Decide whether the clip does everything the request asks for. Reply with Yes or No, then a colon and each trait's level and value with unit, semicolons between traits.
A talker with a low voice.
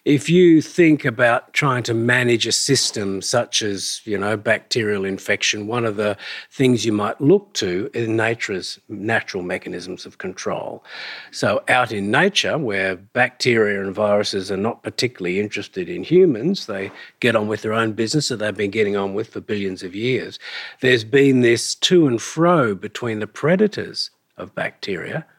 Yes: low, 115 Hz